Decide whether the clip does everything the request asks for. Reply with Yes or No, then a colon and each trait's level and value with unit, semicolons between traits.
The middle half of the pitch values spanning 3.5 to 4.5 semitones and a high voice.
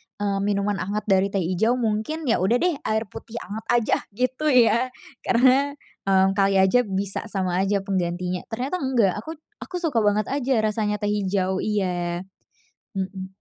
Yes: average, 4.0 semitones; high, 205 Hz